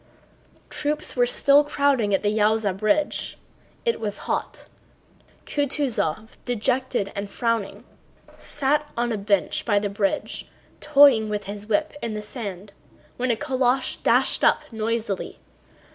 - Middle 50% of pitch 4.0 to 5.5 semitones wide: Yes, average, 4.7 semitones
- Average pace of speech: No, slow, 130 wpm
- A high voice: Yes, high, 225 Hz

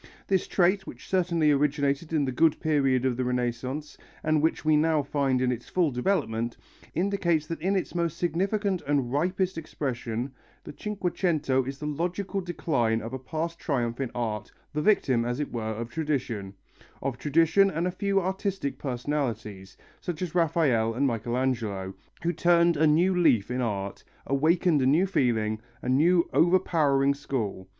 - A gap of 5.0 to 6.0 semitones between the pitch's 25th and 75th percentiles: Yes, wide, 5.6 semitones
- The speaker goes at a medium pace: Yes, average, 165 wpm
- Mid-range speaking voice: Yes, medium, 145 Hz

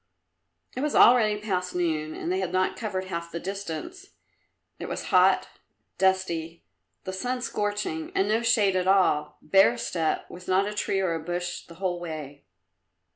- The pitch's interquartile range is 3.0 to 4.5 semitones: Yes, average, 3.4 semitones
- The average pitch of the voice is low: No, medium, 185 Hz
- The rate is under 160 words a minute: No, average, 170 wpm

